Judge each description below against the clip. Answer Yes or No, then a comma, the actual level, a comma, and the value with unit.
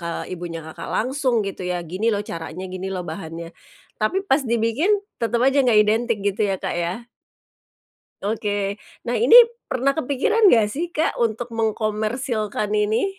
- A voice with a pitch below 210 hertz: No, high, 215 Hz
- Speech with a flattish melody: No, average, 4.5 semitones